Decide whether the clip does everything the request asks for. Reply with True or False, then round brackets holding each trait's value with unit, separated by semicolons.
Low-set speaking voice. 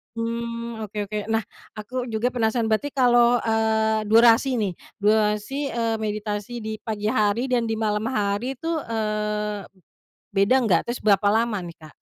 False (220 Hz)